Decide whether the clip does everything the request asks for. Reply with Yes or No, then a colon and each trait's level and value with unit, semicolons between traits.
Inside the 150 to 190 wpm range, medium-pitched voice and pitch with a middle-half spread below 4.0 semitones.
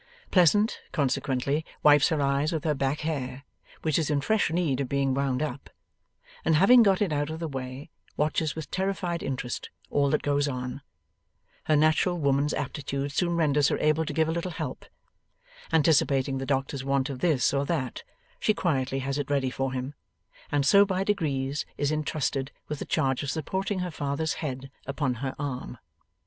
Yes: average, 180 wpm; medium, 145 Hz; average, 2.9 semitones